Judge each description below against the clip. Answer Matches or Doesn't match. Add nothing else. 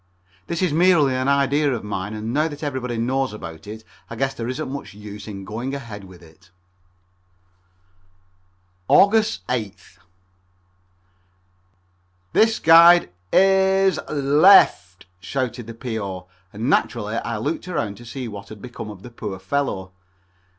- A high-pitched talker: Doesn't match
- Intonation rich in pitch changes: Matches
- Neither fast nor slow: Matches